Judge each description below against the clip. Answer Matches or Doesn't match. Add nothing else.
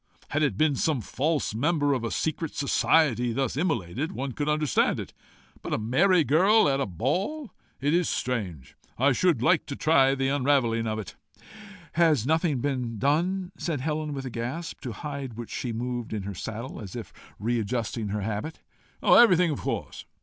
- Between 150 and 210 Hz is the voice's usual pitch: Doesn't match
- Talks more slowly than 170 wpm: Doesn't match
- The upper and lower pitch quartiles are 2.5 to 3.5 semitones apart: Doesn't match